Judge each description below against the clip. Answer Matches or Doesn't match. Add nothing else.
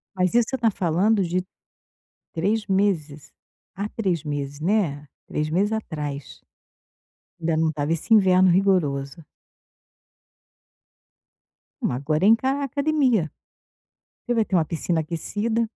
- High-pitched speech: Doesn't match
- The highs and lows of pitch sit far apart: Matches